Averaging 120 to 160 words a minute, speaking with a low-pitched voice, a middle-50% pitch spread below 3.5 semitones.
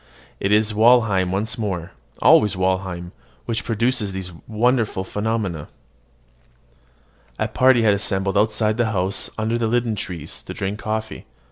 Yes: slow, 135 wpm; low, 105 Hz; average, 2.9 semitones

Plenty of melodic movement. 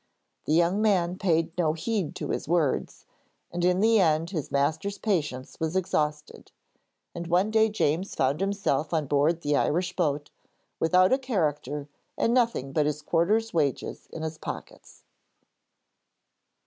No: average, 4.2 semitones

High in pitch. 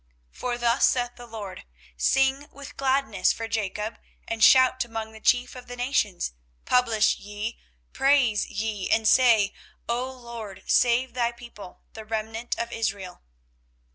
Yes: high, 235 Hz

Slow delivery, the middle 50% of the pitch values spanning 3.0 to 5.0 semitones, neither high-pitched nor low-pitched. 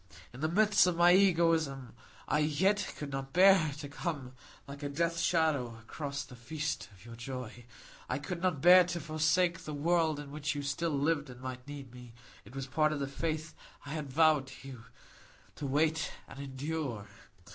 No: average, 185 wpm; average, 3.5 semitones; medium, 145 Hz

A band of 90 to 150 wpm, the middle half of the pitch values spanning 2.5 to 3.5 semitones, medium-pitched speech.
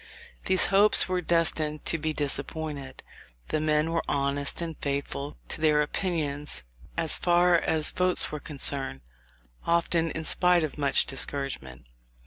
Yes: slow, 135 wpm; average, 2.9 semitones; medium, 155 Hz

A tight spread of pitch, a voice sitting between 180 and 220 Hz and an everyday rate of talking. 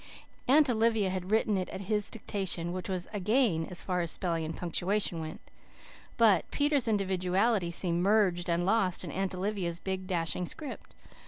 No: average, 3.3 semitones; high, 190 Hz; average, 170 wpm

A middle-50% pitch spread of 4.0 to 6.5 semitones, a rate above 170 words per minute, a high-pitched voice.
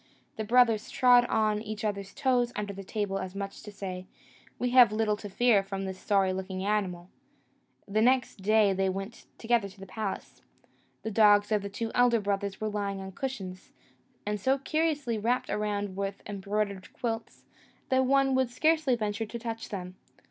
No: average, 3.3 semitones; average, 180 wpm; high, 210 Hz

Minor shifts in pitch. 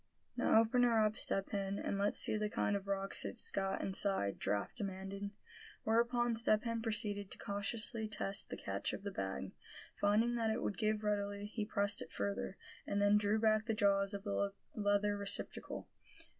Yes: narrow, 1.7 semitones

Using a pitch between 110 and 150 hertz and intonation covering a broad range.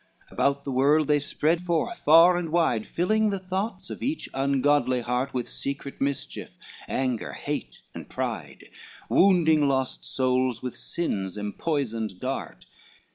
No: medium, 140 Hz; average, 4.9 semitones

